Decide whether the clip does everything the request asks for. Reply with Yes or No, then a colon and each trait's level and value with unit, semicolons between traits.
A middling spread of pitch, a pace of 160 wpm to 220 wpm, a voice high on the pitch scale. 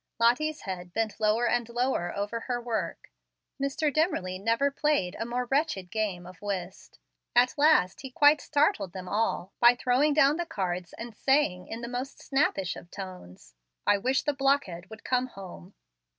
No: wide, 6.3 semitones; average, 170 wpm; high, 235 Hz